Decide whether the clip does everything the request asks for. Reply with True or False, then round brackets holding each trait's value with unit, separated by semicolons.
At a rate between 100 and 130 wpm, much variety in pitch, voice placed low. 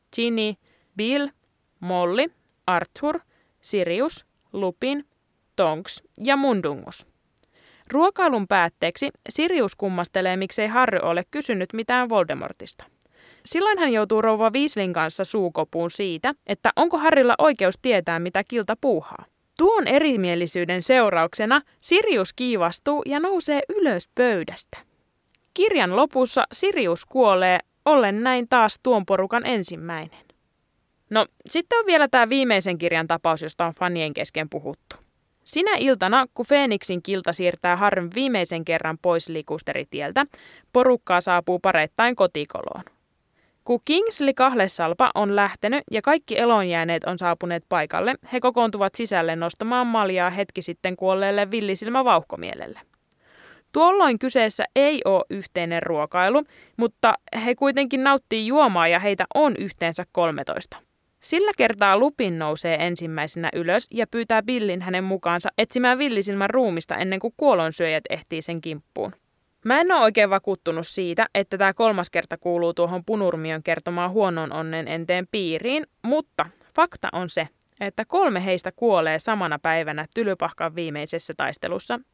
False (125 wpm; 6.8 semitones; 200 Hz)